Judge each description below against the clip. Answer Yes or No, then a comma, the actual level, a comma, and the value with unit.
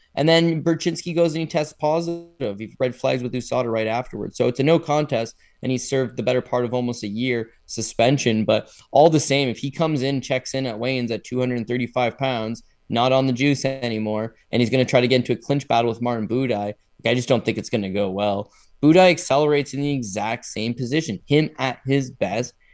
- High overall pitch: No, low, 125 Hz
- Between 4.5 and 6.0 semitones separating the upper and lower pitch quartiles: No, average, 3.6 semitones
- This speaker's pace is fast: Yes, fast, 225 wpm